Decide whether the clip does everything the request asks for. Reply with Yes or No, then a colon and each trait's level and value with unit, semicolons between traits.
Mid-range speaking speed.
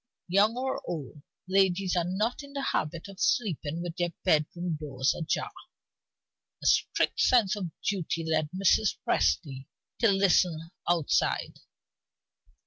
No: slow, 130 wpm